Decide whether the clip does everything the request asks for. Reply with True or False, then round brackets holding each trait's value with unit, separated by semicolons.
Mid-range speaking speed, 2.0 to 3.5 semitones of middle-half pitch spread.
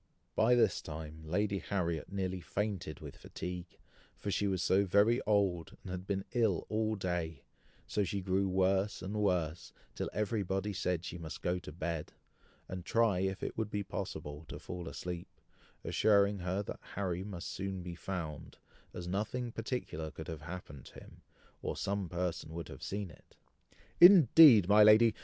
True (170 wpm; 3.0 semitones)